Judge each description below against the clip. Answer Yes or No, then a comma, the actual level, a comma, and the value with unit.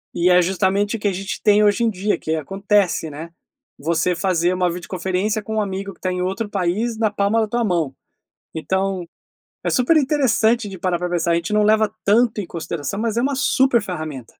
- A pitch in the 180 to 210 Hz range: Yes, high, 195 Hz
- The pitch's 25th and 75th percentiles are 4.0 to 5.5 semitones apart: No, average, 3.4 semitones